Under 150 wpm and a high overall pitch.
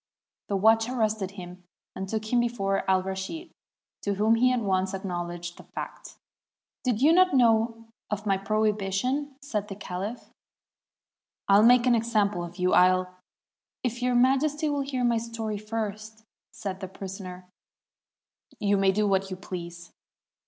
No: average, 155 wpm; high, 210 Hz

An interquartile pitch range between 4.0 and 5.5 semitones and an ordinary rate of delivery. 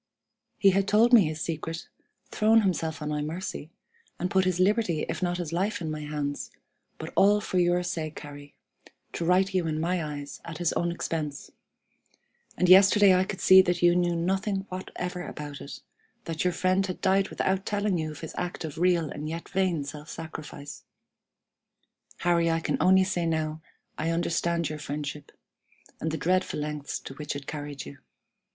No: average, 3.3 semitones; average, 185 wpm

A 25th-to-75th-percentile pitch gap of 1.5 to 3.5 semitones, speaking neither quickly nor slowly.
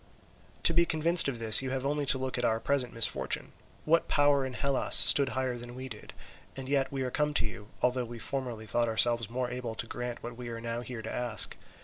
No: narrow, 2.6 semitones; fast, 235 wpm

